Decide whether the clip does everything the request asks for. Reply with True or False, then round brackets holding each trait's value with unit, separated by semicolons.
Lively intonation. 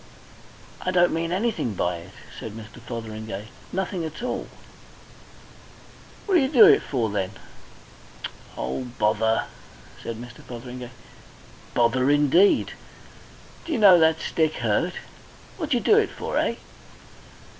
True (8.8 semitones)